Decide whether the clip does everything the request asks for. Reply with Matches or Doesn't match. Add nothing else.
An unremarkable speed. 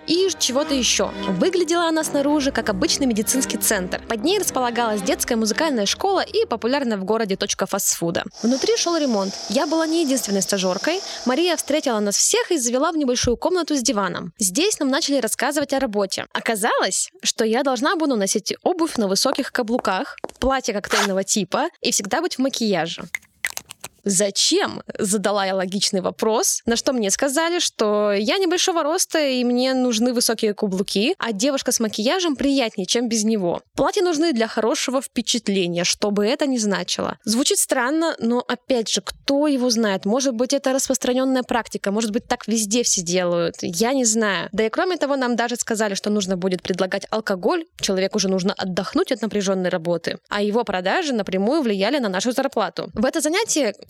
Doesn't match